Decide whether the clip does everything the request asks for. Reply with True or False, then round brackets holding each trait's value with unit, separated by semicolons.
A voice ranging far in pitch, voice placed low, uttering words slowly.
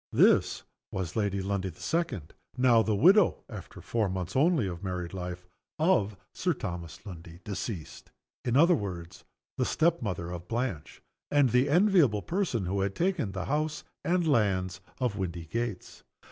False (8.1 semitones; 105 Hz; 155 wpm)